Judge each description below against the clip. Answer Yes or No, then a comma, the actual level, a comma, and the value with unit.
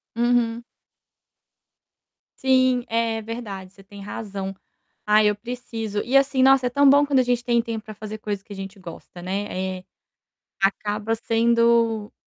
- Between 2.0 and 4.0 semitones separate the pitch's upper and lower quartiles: Yes, average, 3.1 semitones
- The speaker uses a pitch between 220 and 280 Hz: Yes, high, 225 Hz